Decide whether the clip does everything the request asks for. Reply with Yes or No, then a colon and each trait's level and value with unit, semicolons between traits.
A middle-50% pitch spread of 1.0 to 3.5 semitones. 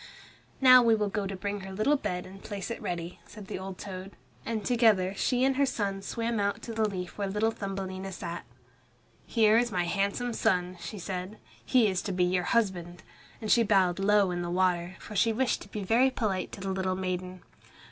Yes: average, 3.1 semitones